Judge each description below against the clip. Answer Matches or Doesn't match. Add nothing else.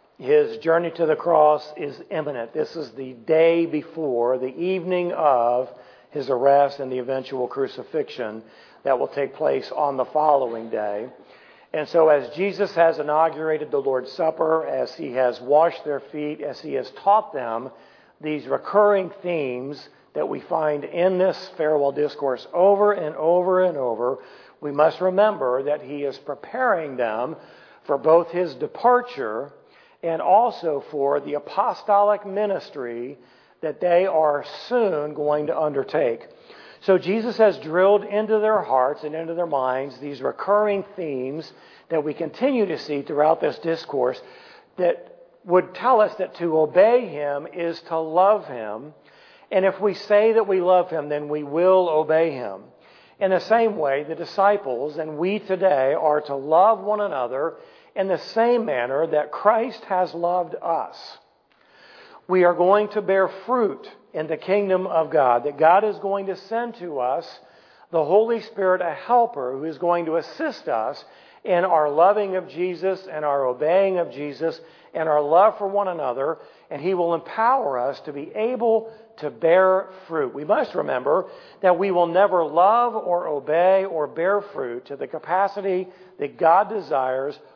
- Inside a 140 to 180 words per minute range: Matches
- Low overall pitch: Doesn't match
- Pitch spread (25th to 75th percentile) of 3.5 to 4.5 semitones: Doesn't match